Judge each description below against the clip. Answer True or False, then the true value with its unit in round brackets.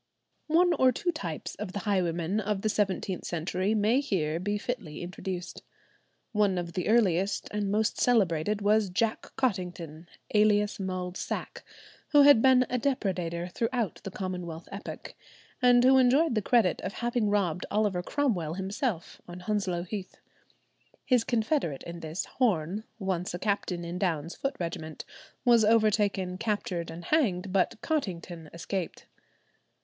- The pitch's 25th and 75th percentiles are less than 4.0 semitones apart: False (4.3 semitones)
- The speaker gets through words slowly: False (145 wpm)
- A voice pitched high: True (195 Hz)